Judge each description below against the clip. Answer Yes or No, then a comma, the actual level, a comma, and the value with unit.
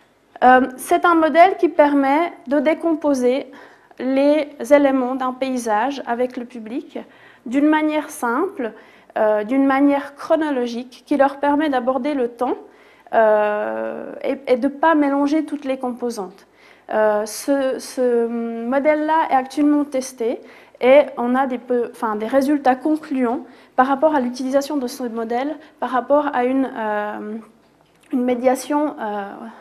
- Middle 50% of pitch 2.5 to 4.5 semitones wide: Yes, average, 3.3 semitones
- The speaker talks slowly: Yes, slow, 140 wpm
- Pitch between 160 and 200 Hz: No, very high, 265 Hz